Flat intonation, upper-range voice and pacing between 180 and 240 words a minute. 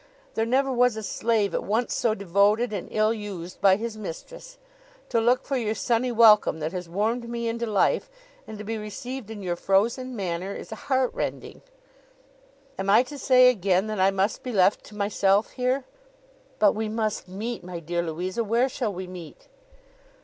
No: average, 3.5 semitones; high, 215 Hz; average, 185 wpm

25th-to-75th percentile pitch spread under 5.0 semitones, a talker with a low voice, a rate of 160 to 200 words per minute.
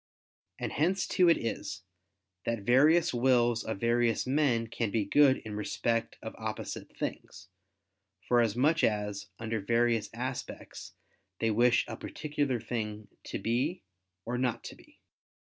No: average, 2.8 semitones; low, 120 Hz; average, 145 wpm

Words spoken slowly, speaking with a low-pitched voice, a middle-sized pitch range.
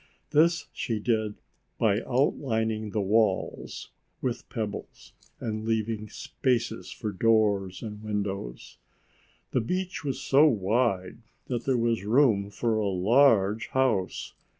Yes: slow, 120 wpm; low, 110 Hz; average, 3.0 semitones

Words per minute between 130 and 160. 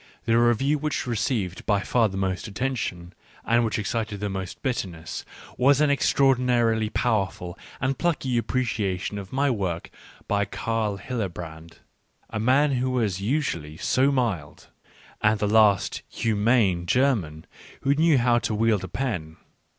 Yes: average, 145 wpm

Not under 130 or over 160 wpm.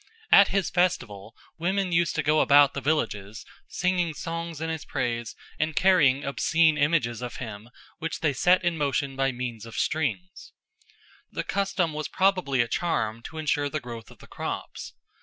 No: average, 170 wpm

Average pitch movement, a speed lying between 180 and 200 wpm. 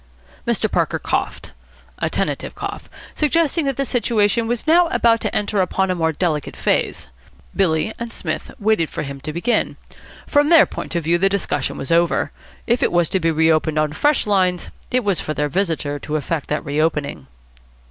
No: wide, 6.6 semitones; average, 185 wpm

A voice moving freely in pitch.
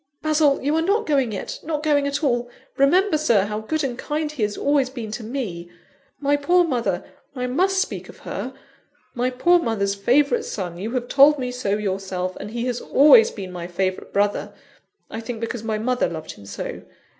Yes: wide, 6.2 semitones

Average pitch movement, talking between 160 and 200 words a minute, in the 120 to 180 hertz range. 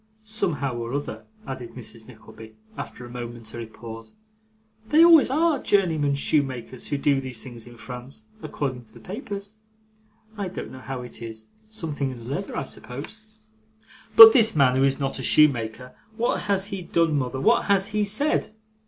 No: wide, 8.6 semitones; average, 170 wpm; medium, 140 Hz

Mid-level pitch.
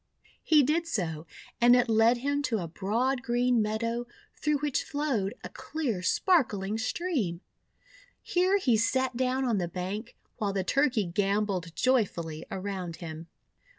No: high, 230 Hz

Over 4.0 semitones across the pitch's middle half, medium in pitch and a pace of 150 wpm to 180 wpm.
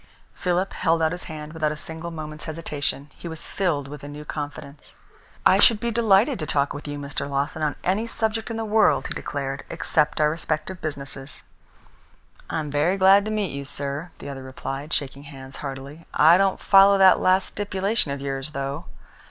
No: average, 4.9 semitones; medium, 155 Hz; average, 190 wpm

